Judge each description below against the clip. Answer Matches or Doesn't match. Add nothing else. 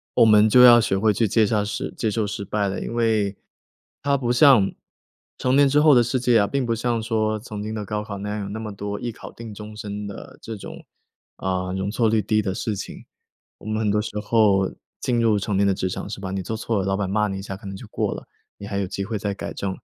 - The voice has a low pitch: Matches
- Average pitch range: Doesn't match